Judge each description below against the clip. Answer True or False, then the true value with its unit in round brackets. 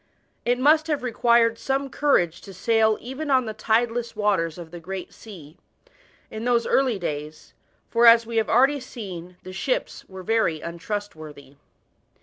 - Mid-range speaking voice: False (220 Hz)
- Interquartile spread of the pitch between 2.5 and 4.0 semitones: False (5.5 semitones)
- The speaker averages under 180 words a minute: True (155 wpm)